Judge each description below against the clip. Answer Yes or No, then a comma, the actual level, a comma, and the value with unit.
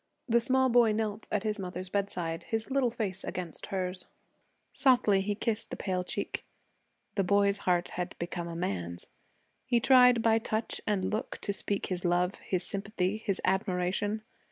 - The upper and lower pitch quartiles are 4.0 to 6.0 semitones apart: No, average, 3.5 semitones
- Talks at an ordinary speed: Yes, average, 165 wpm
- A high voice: Yes, high, 200 Hz